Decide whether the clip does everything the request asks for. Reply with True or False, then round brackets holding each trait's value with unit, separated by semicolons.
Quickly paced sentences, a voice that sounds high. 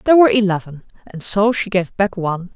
True (210 wpm; 205 Hz)